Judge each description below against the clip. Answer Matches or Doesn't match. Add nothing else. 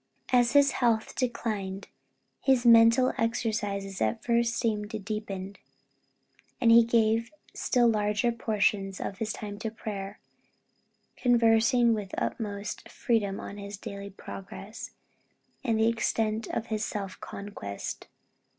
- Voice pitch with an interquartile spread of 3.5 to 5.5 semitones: Doesn't match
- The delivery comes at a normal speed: Doesn't match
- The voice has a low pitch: Doesn't match